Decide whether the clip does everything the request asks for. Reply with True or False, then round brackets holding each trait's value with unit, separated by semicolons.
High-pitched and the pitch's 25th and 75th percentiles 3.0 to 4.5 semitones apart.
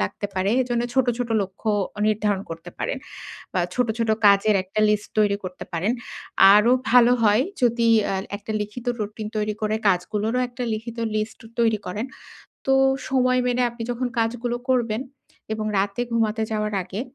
False (215 Hz; 2.6 semitones)